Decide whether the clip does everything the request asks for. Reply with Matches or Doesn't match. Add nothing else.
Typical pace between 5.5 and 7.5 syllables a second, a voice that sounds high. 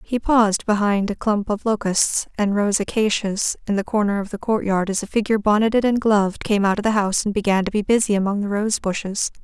Matches